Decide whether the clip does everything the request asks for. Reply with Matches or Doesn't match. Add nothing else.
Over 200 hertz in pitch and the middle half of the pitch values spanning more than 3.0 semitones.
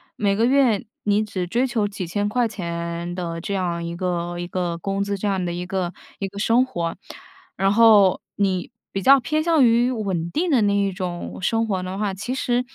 Doesn't match